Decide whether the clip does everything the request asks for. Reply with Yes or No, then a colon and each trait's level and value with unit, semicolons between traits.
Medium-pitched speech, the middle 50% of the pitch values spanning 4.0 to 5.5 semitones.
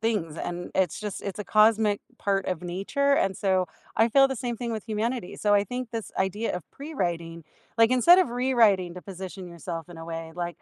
No: high, 200 Hz; average, 4.6 semitones